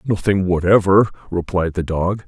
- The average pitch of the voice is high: No, very low, 95 Hz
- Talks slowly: Yes, slow, 130 wpm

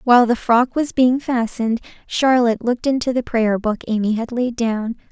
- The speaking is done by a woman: Yes, female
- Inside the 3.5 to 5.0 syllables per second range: No, 5.3 syllables/s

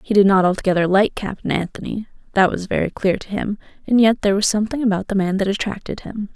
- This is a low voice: No, high, 200 Hz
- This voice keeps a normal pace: No, fast, 215 wpm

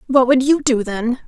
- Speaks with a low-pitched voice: No, very high, 250 Hz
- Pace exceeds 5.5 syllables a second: No, 4.6 syllables/s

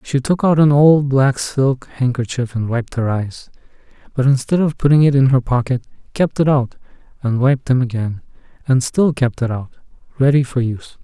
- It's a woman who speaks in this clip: No, male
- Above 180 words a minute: Yes, average, 190 wpm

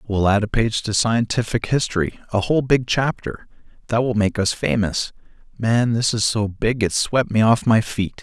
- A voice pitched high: No, low, 110 Hz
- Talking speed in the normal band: Yes, average, 180 wpm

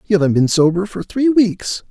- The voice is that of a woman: No, male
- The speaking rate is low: No, fast, 220 wpm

